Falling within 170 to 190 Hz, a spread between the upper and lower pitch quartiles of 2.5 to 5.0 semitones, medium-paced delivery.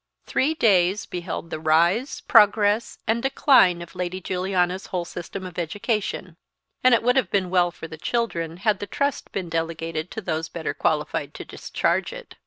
Yes: medium, 185 Hz; average, 4.5 semitones; average, 175 wpm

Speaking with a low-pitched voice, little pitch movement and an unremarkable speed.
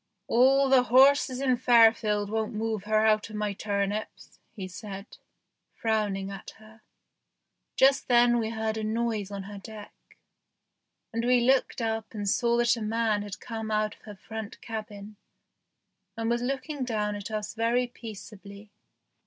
No: high, 220 Hz; narrow, 2.3 semitones; average, 155 wpm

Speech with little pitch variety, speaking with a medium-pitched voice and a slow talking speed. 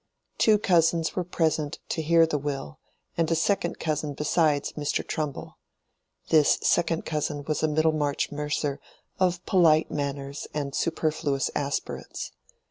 Yes: narrow, 2.2 semitones; medium, 155 Hz; slow, 130 wpm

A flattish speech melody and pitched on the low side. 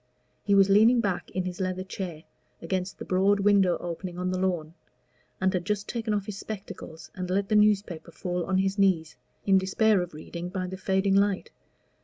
No: narrow, 1.9 semitones; high, 190 Hz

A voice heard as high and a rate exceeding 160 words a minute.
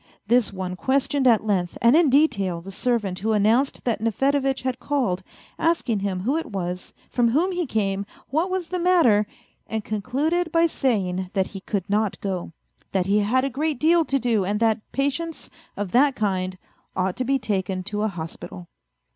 Yes: high, 225 Hz; average, 185 wpm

